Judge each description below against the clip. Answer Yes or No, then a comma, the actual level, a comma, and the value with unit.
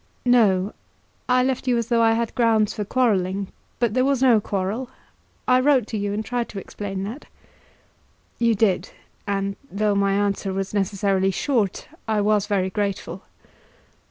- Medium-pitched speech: No, high, 210 Hz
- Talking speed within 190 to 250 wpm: No, average, 160 wpm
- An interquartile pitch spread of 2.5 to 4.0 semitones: Yes, average, 3.2 semitones